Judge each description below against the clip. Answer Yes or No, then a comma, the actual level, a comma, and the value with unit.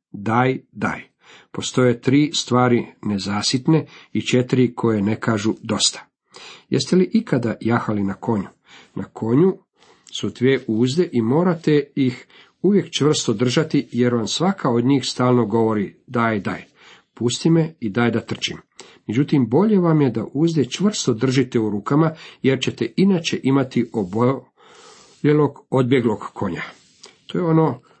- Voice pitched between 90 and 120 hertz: No, low, 130 Hz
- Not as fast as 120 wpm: No, average, 135 wpm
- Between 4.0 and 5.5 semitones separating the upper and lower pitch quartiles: Yes, average, 4.6 semitones